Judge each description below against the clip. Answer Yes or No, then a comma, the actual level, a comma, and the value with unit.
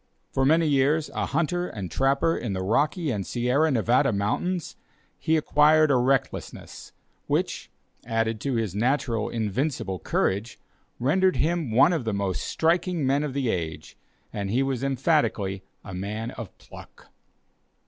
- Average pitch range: No, wide, 6.1 semitones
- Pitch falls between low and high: No, low, 130 Hz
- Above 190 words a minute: No, average, 150 wpm